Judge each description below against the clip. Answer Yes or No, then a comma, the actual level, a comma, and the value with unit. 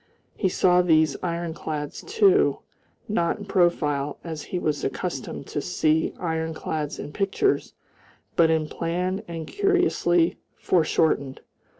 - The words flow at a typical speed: No, slow, 115 wpm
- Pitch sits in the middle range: Yes, medium, 165 Hz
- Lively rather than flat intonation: No, average, 2.8 semitones